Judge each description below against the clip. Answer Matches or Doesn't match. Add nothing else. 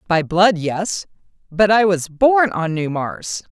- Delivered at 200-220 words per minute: Doesn't match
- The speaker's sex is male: Doesn't match